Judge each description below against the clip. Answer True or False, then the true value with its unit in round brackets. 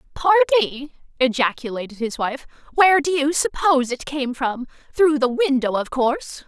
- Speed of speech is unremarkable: True (150 wpm)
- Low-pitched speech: False (280 Hz)